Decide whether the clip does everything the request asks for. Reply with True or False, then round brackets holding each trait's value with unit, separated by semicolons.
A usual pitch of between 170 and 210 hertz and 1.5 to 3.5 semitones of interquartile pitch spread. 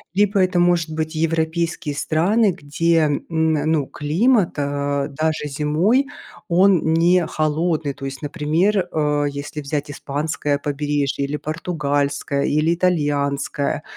False (155 Hz; 2.9 semitones)